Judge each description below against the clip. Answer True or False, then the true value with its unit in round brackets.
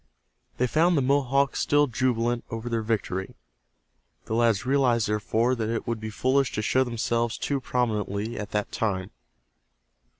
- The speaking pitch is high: False (115 Hz)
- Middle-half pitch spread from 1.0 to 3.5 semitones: True (2.9 semitones)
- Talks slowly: False (155 wpm)